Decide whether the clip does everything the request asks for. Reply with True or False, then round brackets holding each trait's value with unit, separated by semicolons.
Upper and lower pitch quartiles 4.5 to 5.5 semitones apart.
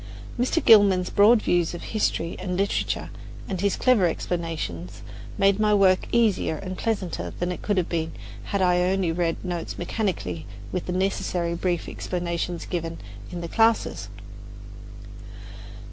False (2.8 semitones)